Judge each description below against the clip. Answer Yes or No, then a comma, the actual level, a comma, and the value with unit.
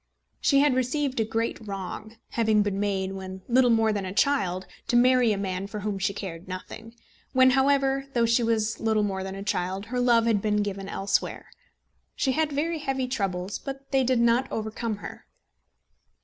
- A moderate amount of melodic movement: Yes, average, 4.5 semitones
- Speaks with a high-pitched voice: Yes, high, 225 Hz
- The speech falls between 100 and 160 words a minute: No, average, 190 wpm